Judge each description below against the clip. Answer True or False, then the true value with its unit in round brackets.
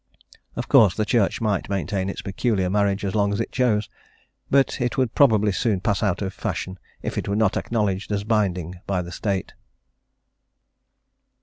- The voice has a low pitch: True (100 Hz)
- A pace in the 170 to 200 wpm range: True (175 wpm)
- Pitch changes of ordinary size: False (2.3 semitones)